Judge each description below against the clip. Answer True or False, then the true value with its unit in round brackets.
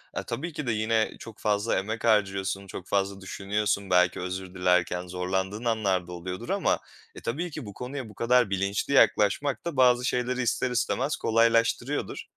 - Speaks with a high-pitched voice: False (105 Hz)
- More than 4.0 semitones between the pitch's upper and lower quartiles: True (4.4 semitones)